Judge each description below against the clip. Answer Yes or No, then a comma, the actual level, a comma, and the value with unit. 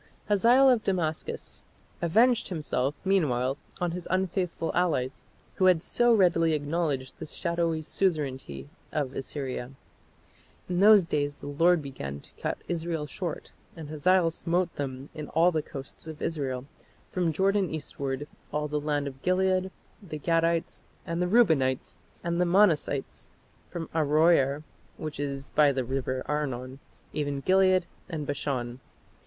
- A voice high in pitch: No, medium, 160 Hz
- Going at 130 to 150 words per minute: Yes, average, 140 wpm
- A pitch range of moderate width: Yes, average, 4.2 semitones